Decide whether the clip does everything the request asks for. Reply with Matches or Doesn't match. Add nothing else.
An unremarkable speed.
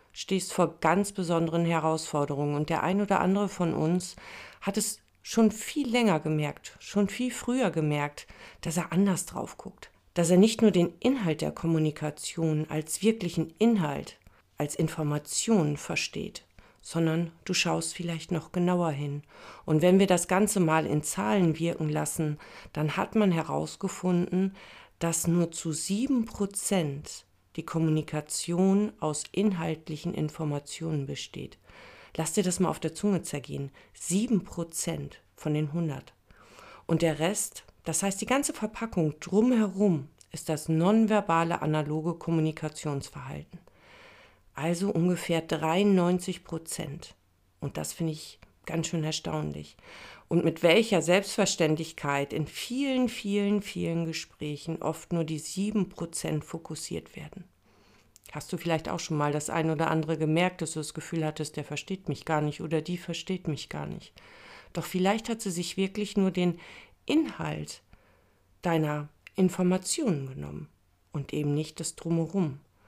Matches